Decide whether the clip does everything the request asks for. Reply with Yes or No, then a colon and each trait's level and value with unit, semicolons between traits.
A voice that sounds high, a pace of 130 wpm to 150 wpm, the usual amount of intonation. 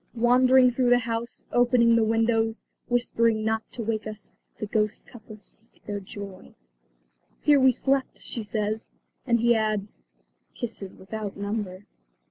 No: high, 225 Hz; average, 140 wpm; narrow, 2.1 semitones